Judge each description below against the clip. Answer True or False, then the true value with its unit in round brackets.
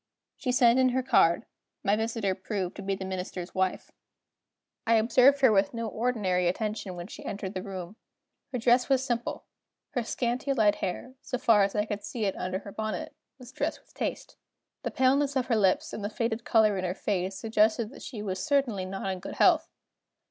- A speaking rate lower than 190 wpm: False (200 wpm)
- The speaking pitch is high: True (215 Hz)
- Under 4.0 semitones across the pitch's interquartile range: False (4.3 semitones)